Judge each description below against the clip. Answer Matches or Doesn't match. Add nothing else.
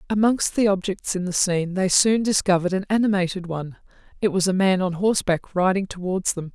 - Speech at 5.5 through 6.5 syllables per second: Matches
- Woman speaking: Matches